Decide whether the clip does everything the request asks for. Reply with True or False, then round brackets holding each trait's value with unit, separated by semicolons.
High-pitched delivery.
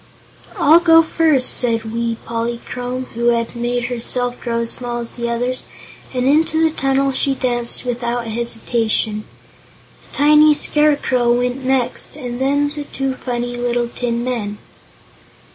True (245 Hz)